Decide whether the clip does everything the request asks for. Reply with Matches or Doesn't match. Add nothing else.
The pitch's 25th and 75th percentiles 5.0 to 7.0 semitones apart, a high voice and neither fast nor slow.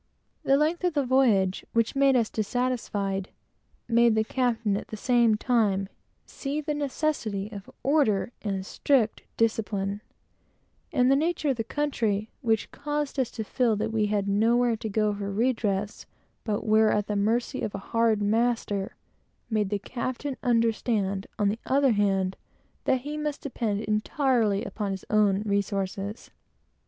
Doesn't match